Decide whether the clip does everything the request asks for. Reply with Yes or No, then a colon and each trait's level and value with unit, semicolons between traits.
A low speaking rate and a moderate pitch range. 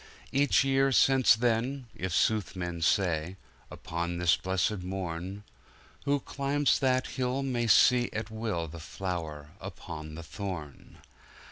No: slow, 125 wpm; wide, 6.7 semitones